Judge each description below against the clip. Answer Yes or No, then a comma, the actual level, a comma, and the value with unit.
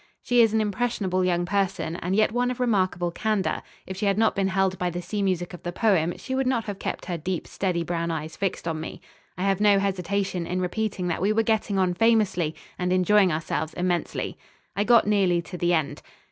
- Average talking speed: No, fast, 220 wpm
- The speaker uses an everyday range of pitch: Yes, average, 3.0 semitones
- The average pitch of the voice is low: No, high, 190 Hz